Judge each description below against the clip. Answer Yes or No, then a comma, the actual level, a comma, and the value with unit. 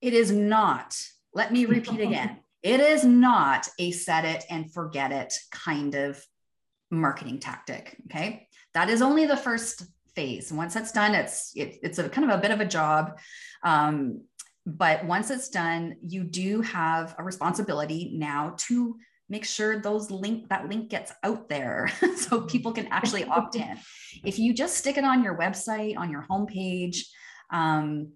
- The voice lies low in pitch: No, high, 200 Hz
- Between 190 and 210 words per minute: No, average, 170 wpm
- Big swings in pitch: Yes, wide, 6.1 semitones